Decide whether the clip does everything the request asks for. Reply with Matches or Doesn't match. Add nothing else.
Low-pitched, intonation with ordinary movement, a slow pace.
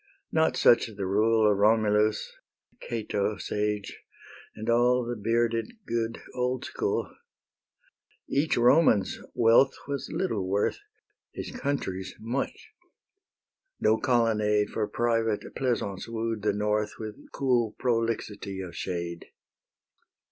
Doesn't match